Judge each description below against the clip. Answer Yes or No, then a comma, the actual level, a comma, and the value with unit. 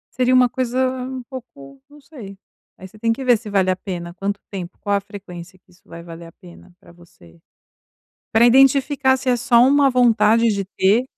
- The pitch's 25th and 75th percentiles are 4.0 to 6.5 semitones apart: Yes, wide, 5.6 semitones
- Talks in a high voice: Yes, high, 215 Hz